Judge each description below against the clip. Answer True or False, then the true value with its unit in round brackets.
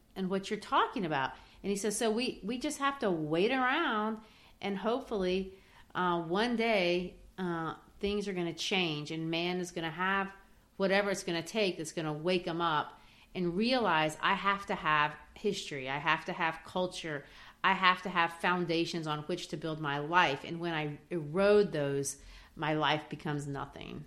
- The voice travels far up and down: False (3.8 semitones)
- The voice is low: False (180 Hz)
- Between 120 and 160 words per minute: False (190 wpm)